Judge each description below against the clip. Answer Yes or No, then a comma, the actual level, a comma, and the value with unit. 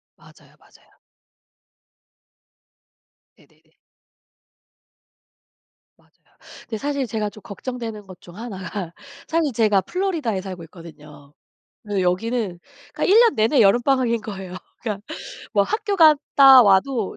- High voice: Yes, high, 220 Hz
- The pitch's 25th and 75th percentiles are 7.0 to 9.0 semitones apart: No, wide, 5.8 semitones